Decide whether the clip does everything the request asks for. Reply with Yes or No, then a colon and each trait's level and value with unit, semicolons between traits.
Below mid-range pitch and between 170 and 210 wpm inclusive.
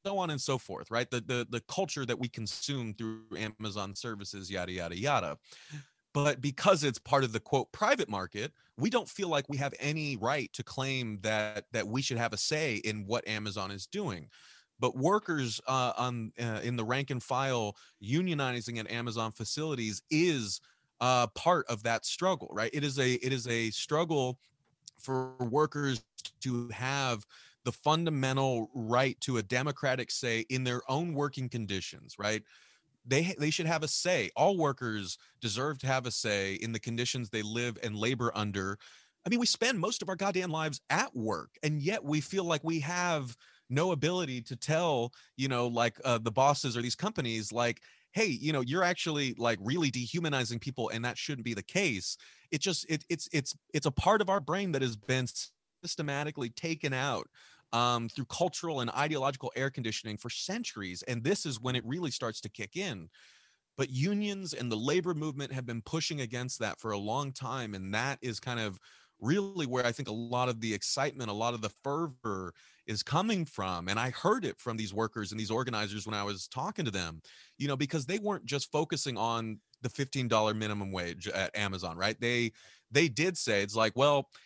Yes: low, 125 Hz; average, 195 wpm